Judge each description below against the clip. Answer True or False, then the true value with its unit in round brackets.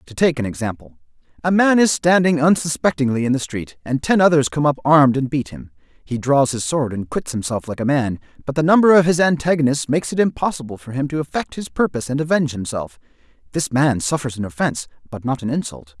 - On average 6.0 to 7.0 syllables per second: True (6.2 syllables/s)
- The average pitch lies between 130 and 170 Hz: True (140 Hz)